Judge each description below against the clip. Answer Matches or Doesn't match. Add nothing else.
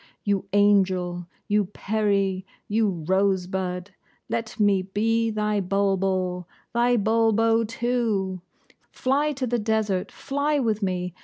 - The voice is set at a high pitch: Matches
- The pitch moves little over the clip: Doesn't match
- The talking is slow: Matches